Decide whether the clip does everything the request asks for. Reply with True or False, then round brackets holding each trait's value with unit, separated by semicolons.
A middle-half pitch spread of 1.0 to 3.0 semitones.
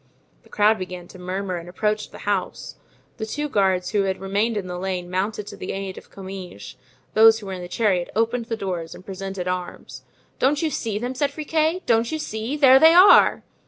False (4.0 semitones)